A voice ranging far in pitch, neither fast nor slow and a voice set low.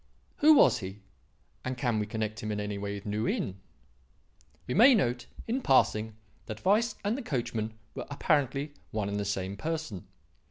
Yes: wide, 6.8 semitones; average, 175 wpm; low, 110 Hz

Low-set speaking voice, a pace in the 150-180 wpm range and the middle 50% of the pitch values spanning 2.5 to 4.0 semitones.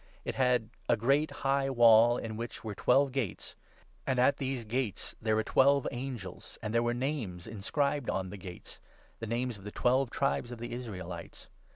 No: low, 120 Hz; average, 190 wpm; average, 3.6 semitones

